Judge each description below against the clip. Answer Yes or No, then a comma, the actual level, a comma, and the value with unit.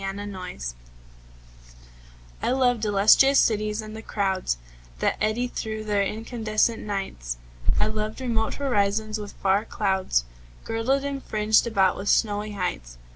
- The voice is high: Yes, high, 215 Hz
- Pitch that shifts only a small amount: Yes, narrow, 2.1 semitones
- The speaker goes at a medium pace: No, slow, 130 wpm